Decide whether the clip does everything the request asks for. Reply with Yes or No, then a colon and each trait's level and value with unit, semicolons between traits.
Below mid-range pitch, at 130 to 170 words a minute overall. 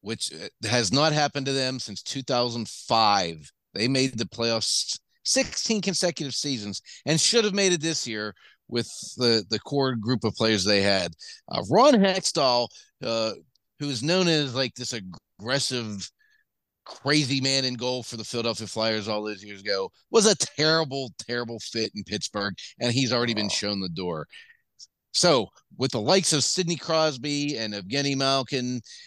Yes: low, 125 Hz; average, 160 wpm